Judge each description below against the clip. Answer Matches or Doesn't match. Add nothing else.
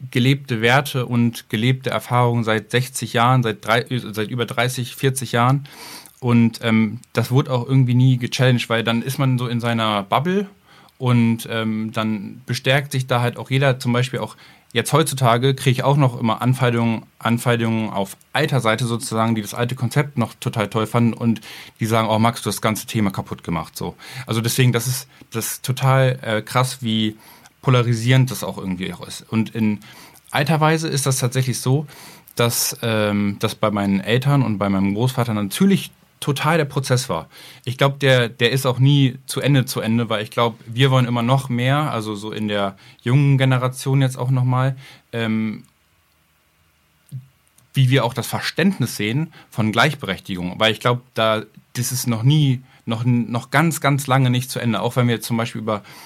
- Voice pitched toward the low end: Matches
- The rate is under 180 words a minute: Doesn't match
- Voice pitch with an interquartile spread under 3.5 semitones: Matches